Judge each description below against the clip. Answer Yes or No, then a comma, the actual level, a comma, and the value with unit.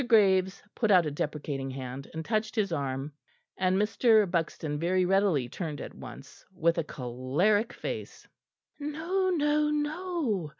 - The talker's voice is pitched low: No, medium, 185 Hz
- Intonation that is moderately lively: No, wide, 7.2 semitones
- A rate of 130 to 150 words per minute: Yes, average, 140 wpm